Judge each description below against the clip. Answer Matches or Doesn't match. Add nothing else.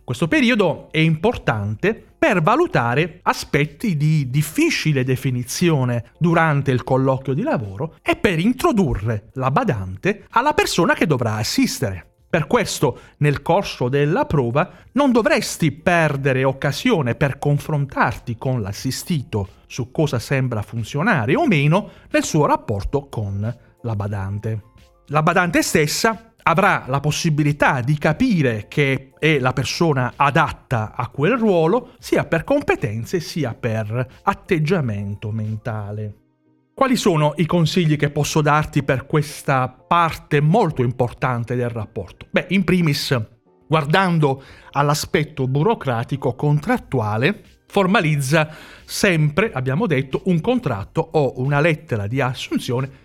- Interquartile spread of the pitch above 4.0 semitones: Matches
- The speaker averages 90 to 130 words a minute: Matches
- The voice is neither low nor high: Matches